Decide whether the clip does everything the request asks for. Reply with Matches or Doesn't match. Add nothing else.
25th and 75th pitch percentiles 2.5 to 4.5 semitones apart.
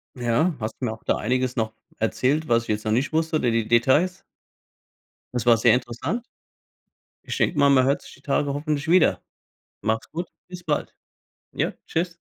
Doesn't match